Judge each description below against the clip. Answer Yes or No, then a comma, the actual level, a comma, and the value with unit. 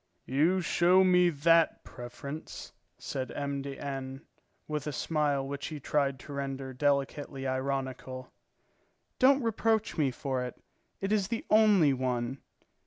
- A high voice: No, medium, 140 Hz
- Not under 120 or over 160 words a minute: Yes, slow, 135 wpm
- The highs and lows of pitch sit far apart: No, average, 4.3 semitones